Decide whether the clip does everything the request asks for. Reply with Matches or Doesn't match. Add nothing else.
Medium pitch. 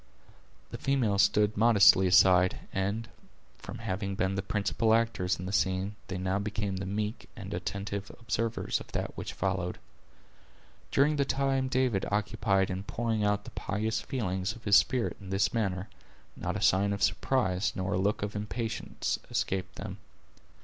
Doesn't match